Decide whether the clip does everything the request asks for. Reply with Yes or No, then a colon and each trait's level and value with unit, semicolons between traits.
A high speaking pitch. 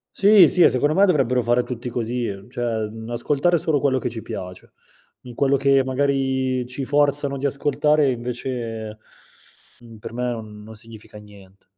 No: low, 125 Hz